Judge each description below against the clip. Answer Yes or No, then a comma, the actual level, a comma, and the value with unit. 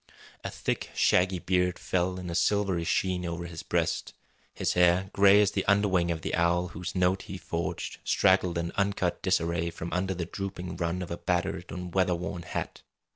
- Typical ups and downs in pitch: No, narrow, 1.6 semitones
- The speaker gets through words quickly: No, average, 180 wpm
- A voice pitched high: No, very low, 90 Hz